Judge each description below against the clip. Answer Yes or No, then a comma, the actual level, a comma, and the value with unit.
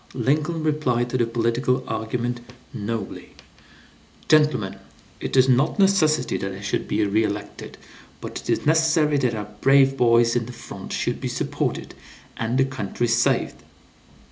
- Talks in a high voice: No, low, 120 Hz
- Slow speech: No, average, 150 wpm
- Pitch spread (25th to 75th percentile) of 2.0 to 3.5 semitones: No, average, 4.2 semitones